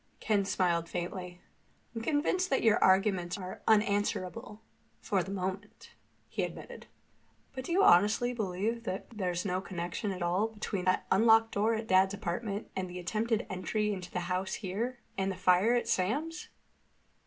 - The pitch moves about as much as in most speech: Yes, average, 3.5 semitones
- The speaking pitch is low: No, high, 200 Hz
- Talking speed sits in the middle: Yes, average, 150 wpm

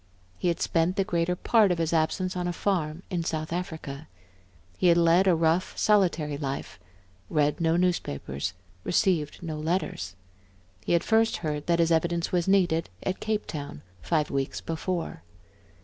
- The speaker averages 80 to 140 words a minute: No, average, 165 wpm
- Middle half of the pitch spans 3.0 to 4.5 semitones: No, narrow, 2.5 semitones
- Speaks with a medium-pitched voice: Yes, medium, 170 Hz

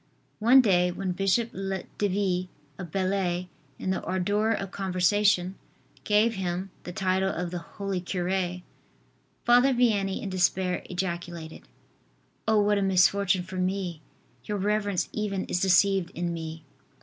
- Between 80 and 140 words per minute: Yes, slow, 135 wpm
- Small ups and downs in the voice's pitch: Yes, narrow, 2.0 semitones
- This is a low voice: No, high, 190 Hz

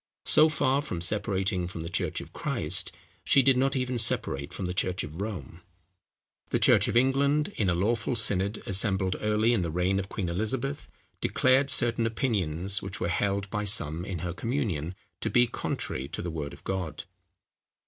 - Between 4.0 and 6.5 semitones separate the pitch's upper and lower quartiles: Yes, average, 5.2 semitones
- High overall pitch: No, low, 100 Hz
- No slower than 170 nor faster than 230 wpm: Yes, average, 180 wpm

